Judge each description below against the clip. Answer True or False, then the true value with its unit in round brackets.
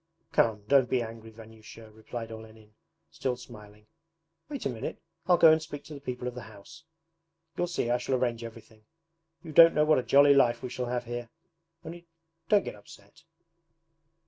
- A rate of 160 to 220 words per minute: True (180 wpm)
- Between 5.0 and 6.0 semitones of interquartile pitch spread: False (4.1 semitones)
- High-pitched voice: False (120 Hz)